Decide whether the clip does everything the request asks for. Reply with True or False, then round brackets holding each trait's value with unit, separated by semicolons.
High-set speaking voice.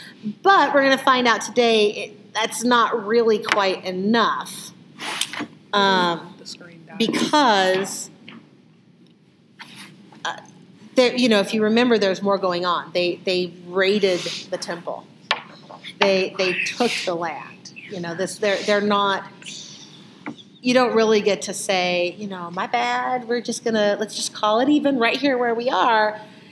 True (205 Hz)